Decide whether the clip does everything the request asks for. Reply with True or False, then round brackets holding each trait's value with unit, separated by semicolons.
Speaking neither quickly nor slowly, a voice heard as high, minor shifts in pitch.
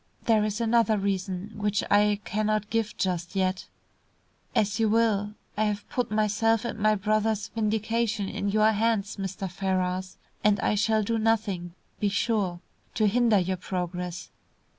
True (150 wpm; 210 Hz; 2.2 semitones)